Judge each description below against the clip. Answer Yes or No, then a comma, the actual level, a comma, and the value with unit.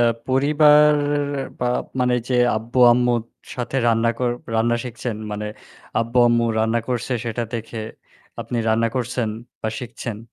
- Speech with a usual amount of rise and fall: No, narrow, 1.6 semitones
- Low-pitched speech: Yes, low, 120 Hz